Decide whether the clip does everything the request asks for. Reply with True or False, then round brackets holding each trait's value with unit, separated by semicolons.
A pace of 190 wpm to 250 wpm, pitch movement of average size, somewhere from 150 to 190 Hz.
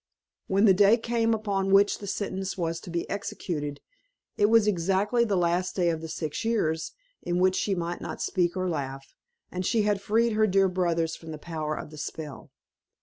True (200 wpm; 3.7 semitones; 185 Hz)